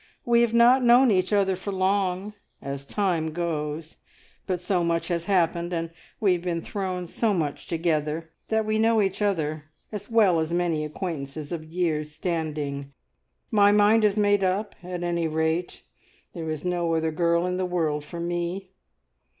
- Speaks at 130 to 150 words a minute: No, average, 170 wpm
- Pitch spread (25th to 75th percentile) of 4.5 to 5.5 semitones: No, average, 3.7 semitones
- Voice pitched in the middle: Yes, medium, 175 Hz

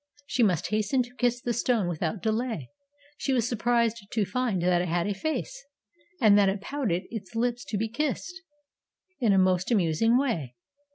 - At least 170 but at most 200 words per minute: Yes, average, 180 wpm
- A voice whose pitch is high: Yes, high, 220 Hz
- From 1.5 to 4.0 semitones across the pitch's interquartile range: No, average, 4.6 semitones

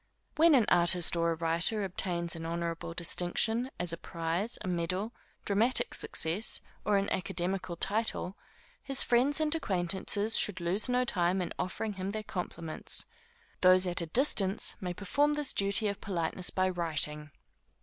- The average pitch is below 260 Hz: Yes, medium, 185 Hz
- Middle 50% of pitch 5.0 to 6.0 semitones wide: No, average, 4.0 semitones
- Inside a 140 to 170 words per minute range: Yes, average, 155 wpm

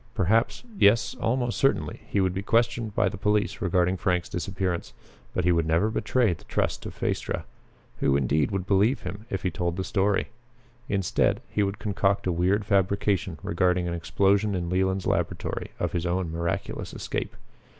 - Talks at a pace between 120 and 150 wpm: No, average, 170 wpm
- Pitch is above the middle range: No, very low, 95 Hz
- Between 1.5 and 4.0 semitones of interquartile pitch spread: Yes, average, 2.8 semitones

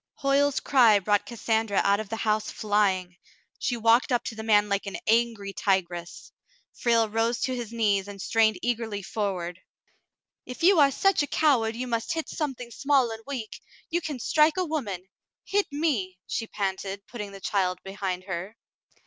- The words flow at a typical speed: Yes, average, 175 wpm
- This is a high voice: Yes, high, 225 Hz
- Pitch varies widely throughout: No, average, 4.1 semitones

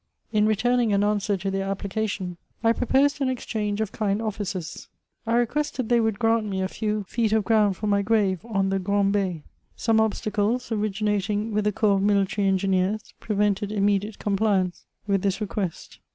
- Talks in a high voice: Yes, high, 210 Hz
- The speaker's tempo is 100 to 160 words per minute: No, average, 170 wpm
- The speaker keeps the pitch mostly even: Yes, narrow, 2.0 semitones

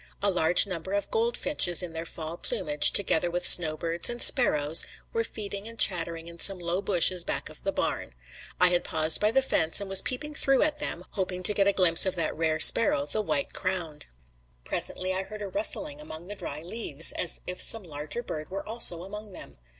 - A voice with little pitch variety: No, average, 4.2 semitones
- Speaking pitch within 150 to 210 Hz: Yes, medium, 185 Hz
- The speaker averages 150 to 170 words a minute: No, fast, 205 wpm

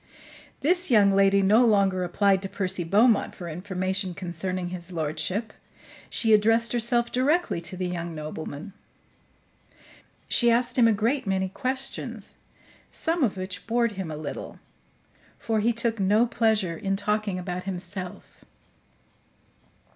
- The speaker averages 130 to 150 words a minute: Yes, slow, 135 wpm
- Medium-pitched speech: No, high, 195 Hz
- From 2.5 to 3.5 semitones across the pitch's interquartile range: No, average, 4.0 semitones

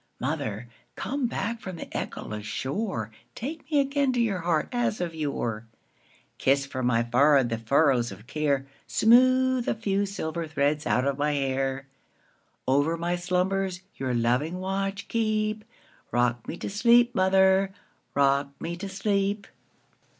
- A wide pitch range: Yes, wide, 7.0 semitones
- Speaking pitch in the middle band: Yes, medium, 170 Hz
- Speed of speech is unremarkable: No, slow, 130 wpm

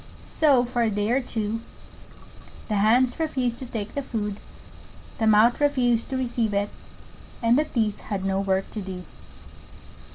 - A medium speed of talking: Yes, average, 160 wpm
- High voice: Yes, high, 230 Hz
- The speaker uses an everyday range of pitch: Yes, average, 3.3 semitones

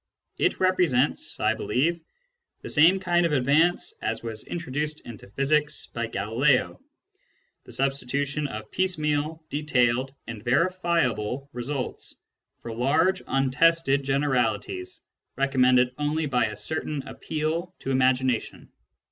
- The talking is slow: Yes, slow, 115 wpm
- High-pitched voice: No, medium, 140 Hz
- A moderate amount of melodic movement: Yes, average, 4.3 semitones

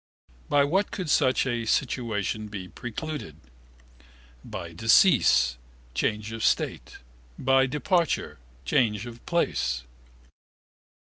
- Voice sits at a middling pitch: No, low, 120 Hz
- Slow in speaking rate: Yes, slow, 100 wpm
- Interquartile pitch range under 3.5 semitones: No, average, 5.3 semitones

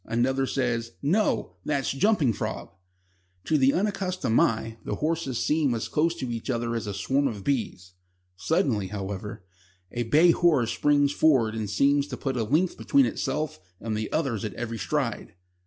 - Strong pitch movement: No, average, 5.0 semitones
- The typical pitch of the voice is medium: No, low, 130 Hz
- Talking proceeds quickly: No, average, 170 wpm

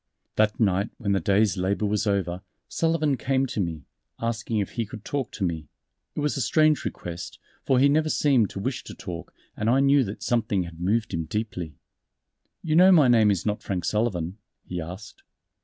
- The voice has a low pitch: Yes, low, 105 Hz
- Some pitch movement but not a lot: No, wide, 6.0 semitones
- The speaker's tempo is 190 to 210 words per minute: Yes, average, 195 wpm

